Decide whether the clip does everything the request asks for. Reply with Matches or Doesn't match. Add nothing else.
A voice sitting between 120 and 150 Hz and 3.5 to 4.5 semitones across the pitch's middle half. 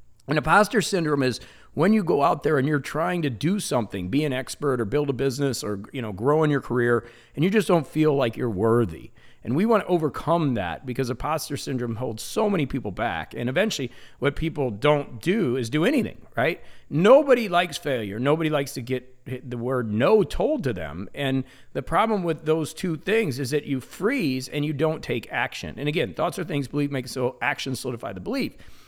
Matches